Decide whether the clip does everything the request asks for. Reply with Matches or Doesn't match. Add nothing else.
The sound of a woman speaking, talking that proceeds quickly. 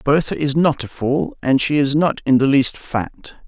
Doesn't match